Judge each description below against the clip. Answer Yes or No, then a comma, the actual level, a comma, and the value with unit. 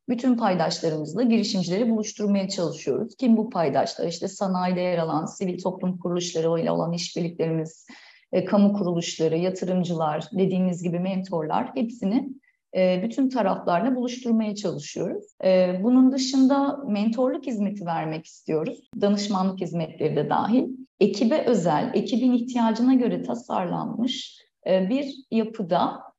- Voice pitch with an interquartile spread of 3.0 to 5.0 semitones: No, wide, 5.5 semitones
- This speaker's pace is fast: No, average, 115 wpm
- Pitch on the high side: Yes, high, 200 Hz